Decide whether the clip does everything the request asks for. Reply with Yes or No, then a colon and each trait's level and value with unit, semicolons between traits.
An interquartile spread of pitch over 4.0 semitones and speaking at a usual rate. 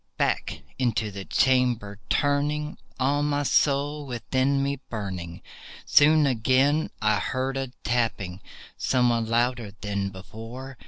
No: average, 4.6 semitones; slow, 115 wpm